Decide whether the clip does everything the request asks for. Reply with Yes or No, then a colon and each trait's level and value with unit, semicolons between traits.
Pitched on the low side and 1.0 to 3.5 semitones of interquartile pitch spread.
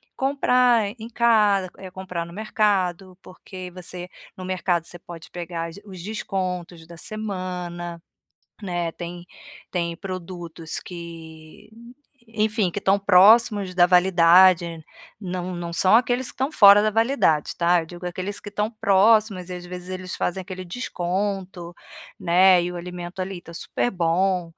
No: medium, 185 Hz; average, 2.7 semitones